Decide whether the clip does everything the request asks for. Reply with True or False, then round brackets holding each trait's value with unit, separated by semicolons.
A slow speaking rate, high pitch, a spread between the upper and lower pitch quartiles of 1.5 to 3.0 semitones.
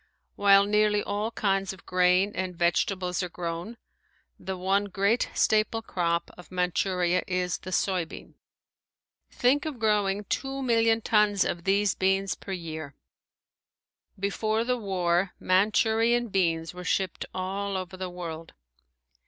True (130 wpm; 195 Hz; 2.7 semitones)